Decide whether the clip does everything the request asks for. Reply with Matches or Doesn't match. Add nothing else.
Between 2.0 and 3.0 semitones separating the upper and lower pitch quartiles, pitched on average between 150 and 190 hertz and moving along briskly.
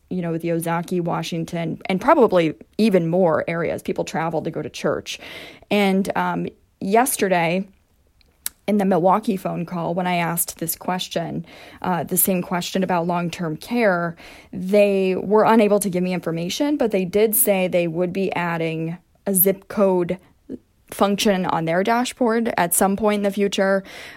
Doesn't match